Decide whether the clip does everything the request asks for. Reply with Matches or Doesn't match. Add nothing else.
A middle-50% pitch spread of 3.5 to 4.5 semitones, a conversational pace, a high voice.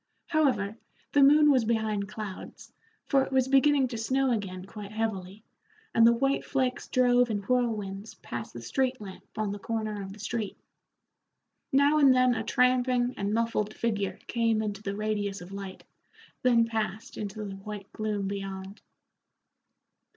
Matches